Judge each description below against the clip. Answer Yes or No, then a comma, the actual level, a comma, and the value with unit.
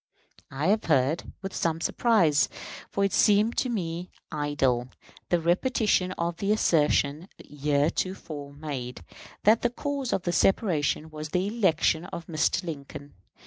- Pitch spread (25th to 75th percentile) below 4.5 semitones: No, average, 5.0 semitones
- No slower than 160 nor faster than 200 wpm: No, average, 140 wpm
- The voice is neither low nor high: Yes, medium, 165 Hz